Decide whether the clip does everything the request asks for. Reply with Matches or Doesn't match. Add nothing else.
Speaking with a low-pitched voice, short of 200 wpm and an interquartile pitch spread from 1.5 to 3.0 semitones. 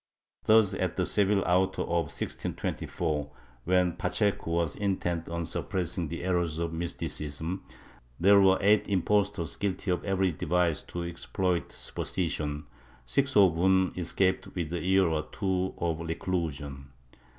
Matches